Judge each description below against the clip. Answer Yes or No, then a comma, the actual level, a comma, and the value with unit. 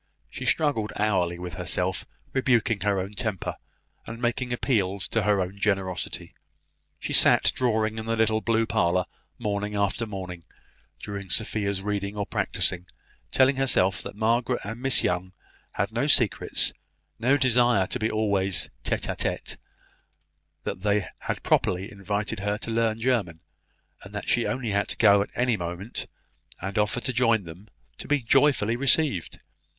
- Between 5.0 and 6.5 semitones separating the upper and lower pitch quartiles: No, average, 3.2 semitones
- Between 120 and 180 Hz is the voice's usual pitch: No, low, 105 Hz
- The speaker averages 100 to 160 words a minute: Yes, average, 155 wpm